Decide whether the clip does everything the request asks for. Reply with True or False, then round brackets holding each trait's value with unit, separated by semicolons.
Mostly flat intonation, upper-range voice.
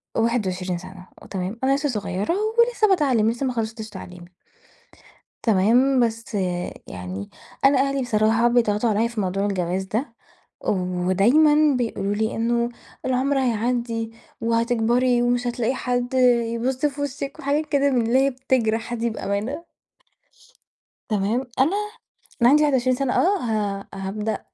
False (3.8 semitones; 235 Hz)